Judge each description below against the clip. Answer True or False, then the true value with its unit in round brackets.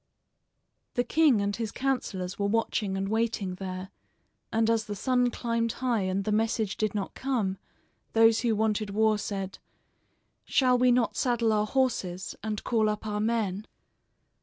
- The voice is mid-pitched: False (220 Hz)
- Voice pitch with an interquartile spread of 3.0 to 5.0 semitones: False (2.6 semitones)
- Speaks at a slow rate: False (160 wpm)